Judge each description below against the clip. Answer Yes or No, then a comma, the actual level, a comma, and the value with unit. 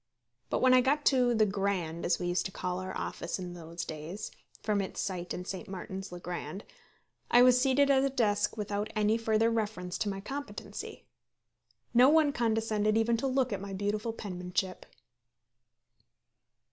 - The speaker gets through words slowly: No, average, 170 wpm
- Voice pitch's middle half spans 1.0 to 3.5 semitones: No, average, 4.3 semitones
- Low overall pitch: No, high, 210 Hz